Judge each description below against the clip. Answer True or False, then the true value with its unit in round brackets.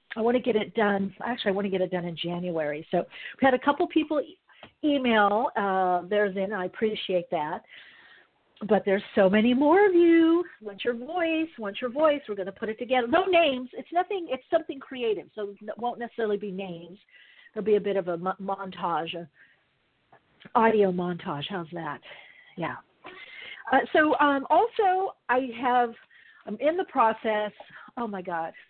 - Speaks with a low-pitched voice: False (220 Hz)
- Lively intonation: True (6.4 semitones)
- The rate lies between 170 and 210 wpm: True (180 wpm)